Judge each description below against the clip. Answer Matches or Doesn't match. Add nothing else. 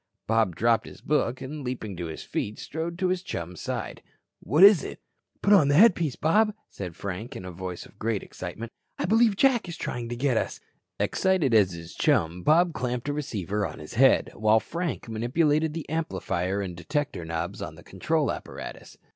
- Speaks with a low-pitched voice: Matches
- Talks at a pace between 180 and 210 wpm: Matches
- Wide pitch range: Matches